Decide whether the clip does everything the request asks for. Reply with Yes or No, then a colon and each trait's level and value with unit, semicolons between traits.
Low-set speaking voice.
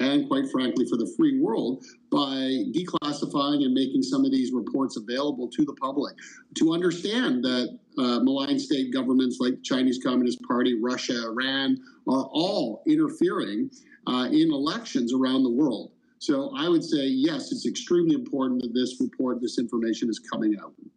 No: very high, 275 Hz